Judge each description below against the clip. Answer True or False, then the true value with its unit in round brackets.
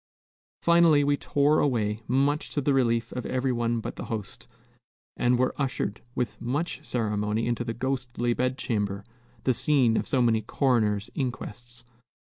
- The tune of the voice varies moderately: True (3.0 semitones)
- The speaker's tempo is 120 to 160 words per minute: True (155 wpm)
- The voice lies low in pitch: True (120 Hz)